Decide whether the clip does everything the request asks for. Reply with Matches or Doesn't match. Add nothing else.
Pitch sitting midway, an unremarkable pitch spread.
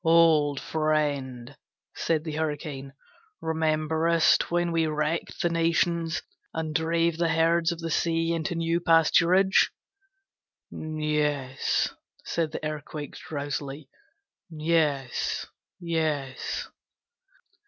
Doesn't match